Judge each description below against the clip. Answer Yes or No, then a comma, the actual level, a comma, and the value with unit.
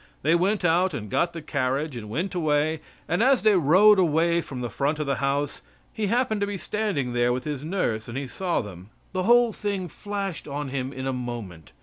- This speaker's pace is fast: Yes, fast, 220 wpm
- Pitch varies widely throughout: Yes, wide, 6.5 semitones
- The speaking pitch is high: No, medium, 155 Hz